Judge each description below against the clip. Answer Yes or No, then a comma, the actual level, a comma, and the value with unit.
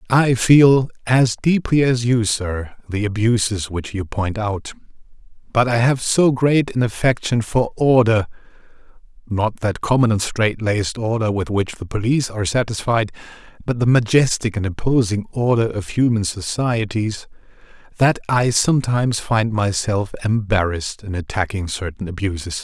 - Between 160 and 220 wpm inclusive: No, average, 140 wpm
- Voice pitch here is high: No, low, 110 Hz